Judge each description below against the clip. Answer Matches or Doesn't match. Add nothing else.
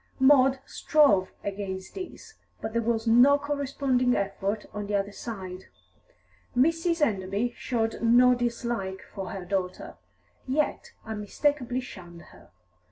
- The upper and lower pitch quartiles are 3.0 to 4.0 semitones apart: Doesn't match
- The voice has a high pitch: Matches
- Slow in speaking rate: Matches